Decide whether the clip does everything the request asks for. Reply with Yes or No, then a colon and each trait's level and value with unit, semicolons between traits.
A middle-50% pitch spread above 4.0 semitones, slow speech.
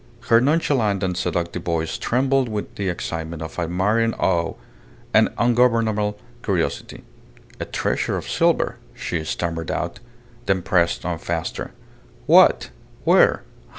Yes: average, 5.2 semitones; slow, 120 wpm